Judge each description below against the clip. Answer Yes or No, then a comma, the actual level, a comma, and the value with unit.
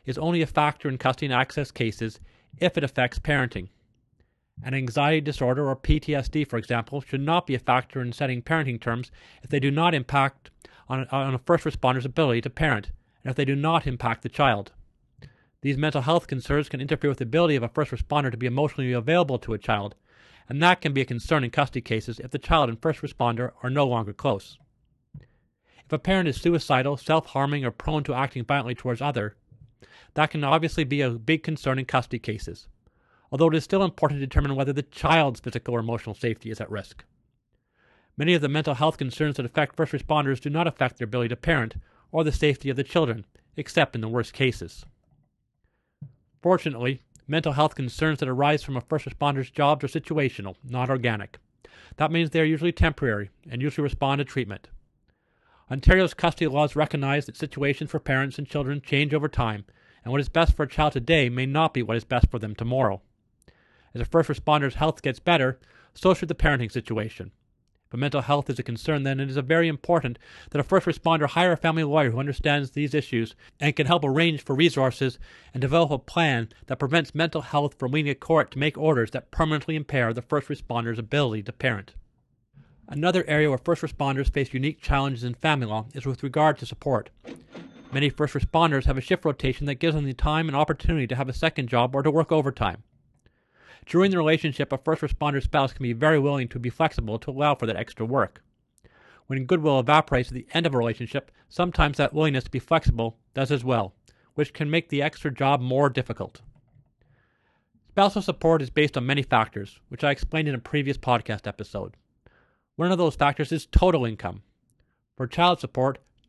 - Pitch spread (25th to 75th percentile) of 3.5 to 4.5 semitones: Yes, average, 3.9 semitones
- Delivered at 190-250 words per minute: Yes, average, 200 wpm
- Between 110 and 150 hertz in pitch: Yes, medium, 140 Hz